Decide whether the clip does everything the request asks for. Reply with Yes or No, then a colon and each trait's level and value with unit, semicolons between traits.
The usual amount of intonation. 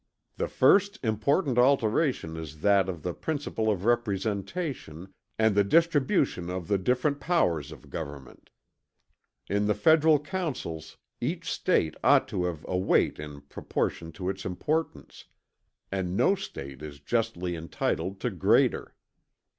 No: wide, 8.6 semitones